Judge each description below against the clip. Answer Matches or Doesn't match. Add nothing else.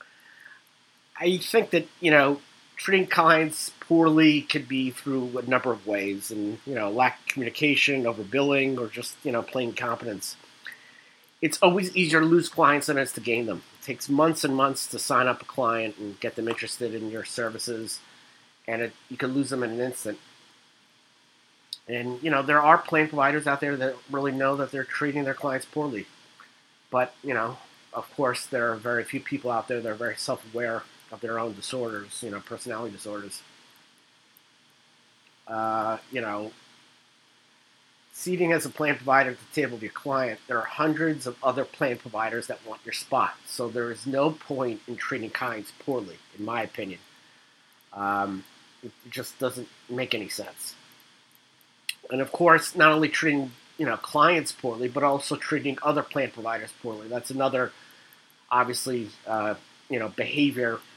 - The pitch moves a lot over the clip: Doesn't match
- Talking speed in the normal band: Matches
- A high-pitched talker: Doesn't match